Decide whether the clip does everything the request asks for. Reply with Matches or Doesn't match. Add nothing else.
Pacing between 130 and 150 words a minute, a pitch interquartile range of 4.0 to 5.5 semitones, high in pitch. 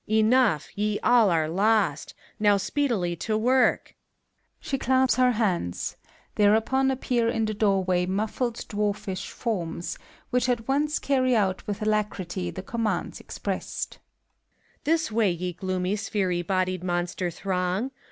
Matches